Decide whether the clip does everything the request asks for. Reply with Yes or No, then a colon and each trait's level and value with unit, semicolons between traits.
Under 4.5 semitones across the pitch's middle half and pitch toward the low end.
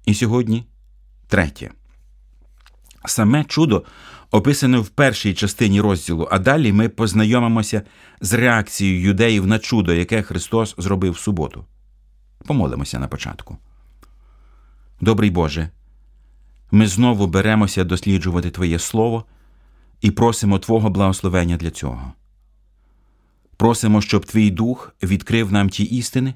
No: average, 4.9 semitones; low, 100 Hz